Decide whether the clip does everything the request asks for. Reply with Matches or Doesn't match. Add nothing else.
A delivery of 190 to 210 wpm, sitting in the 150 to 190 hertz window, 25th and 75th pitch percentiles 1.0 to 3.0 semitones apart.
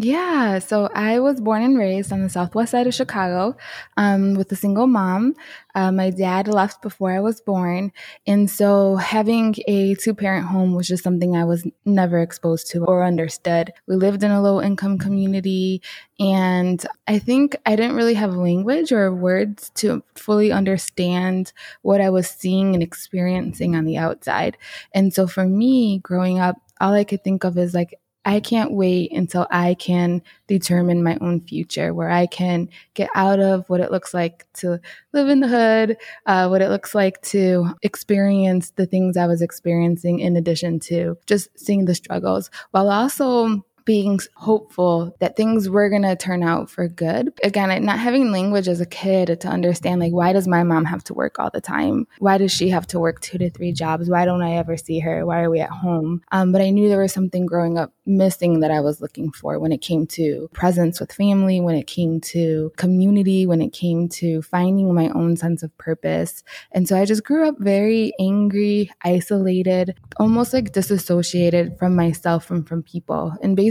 Matches